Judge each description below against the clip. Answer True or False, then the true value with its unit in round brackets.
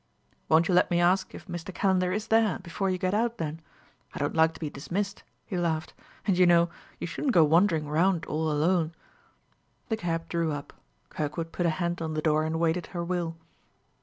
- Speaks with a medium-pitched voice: True (170 Hz)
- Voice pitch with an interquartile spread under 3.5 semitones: True (2.4 semitones)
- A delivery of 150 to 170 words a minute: False (205 wpm)